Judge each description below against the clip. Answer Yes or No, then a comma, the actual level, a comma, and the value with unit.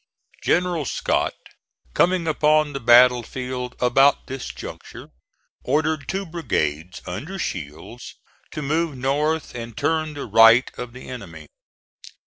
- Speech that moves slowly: Yes, slow, 120 wpm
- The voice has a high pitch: No, low, 135 Hz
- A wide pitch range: No, average, 4.6 semitones